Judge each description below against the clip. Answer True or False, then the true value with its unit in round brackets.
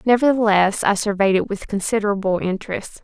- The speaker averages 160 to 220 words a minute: False (140 wpm)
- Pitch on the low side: False (205 Hz)